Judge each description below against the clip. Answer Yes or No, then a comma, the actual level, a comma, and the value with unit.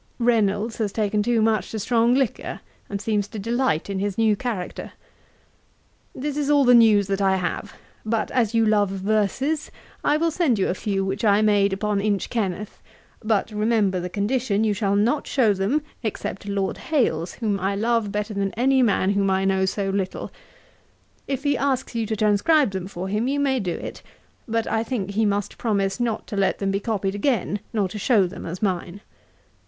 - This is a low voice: No, high, 210 Hz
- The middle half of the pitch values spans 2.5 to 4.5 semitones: Yes, average, 3.0 semitones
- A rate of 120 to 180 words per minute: No, average, 195 wpm